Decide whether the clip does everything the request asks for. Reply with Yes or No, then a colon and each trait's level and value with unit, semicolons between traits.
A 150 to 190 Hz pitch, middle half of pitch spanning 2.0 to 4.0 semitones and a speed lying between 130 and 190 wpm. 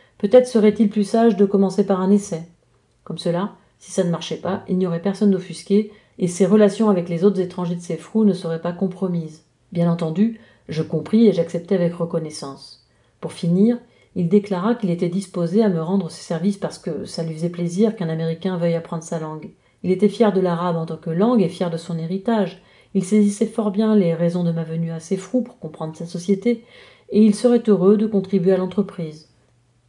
No: medium, 185 Hz; average, 3.6 semitones; average, 210 wpm